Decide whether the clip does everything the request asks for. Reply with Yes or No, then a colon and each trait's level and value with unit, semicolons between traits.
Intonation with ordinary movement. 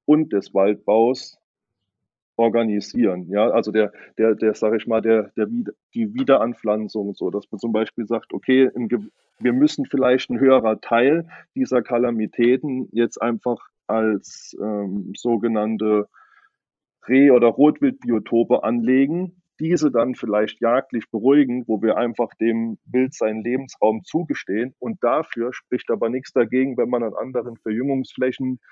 Yes: average, 3.0 semitones